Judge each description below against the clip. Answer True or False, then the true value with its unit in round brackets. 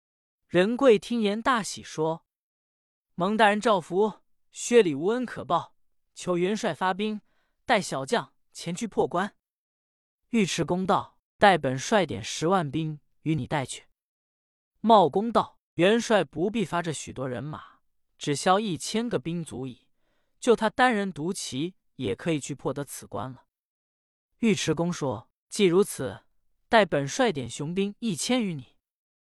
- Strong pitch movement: True (7.5 semitones)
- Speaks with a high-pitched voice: False (180 Hz)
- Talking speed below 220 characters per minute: True (200 characters per minute)